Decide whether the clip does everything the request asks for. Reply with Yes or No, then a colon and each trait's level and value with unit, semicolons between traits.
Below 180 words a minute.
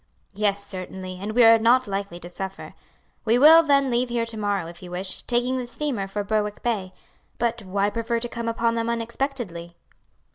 No: average, 190 wpm